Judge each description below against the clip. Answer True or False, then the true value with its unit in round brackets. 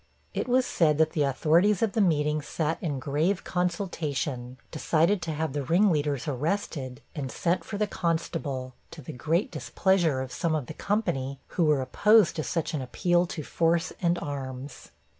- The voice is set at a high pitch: False (160 Hz)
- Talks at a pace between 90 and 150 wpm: False (175 wpm)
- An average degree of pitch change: True (3.9 semitones)